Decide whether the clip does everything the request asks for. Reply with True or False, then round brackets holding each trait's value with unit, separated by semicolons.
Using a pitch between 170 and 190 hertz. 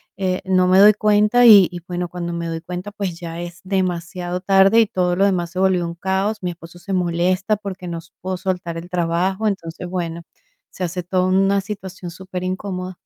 True (185 Hz)